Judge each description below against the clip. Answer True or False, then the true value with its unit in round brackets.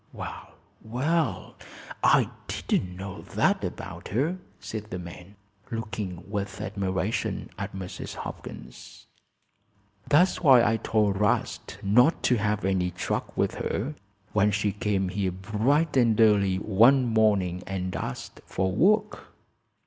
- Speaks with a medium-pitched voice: False (105 Hz)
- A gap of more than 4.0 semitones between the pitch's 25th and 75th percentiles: False (3.4 semitones)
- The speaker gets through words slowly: True (125 wpm)